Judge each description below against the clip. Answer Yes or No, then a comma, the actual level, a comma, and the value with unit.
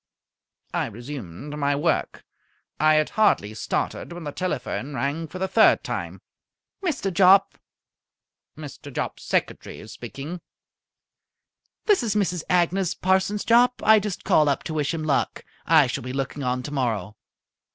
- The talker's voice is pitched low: No, medium, 155 Hz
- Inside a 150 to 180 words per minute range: No, average, 140 wpm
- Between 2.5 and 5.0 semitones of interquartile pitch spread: No, wide, 5.5 semitones